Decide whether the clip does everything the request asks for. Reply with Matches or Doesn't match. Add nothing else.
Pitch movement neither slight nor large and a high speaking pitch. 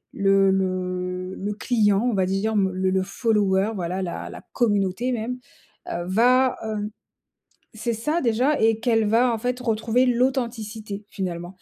Matches